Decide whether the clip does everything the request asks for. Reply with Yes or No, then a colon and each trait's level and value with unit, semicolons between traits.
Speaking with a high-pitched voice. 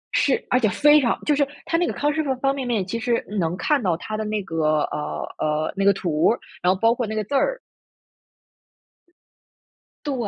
Yes: high, 225 Hz